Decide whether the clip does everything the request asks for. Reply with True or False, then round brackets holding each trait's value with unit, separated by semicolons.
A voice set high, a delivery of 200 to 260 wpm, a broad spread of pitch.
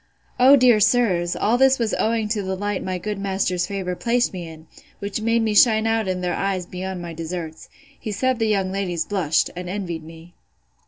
False (195 Hz; 205 wpm; 3.7 semitones)